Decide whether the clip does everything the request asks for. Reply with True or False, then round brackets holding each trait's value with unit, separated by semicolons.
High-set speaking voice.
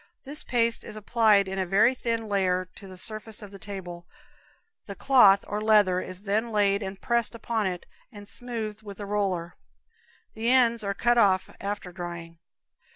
True (205 Hz)